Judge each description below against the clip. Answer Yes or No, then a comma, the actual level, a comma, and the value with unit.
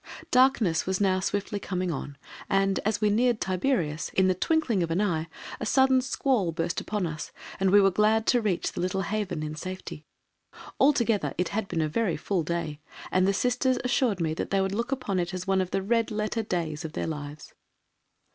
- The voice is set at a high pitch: Yes, high, 195 Hz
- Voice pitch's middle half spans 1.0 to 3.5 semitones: No, average, 4.4 semitones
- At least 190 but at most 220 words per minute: Yes, fast, 205 wpm